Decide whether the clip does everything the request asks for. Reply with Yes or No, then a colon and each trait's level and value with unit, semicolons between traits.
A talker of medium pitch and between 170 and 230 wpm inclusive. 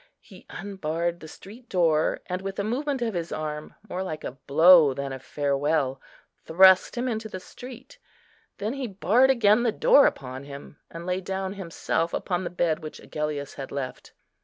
Yes: medium, 175 Hz; average, 180 wpm